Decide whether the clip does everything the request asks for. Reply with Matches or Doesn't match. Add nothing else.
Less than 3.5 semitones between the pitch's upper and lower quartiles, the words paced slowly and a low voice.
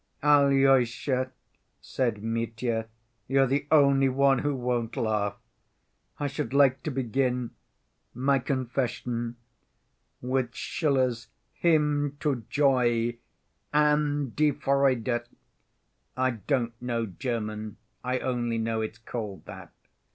Matches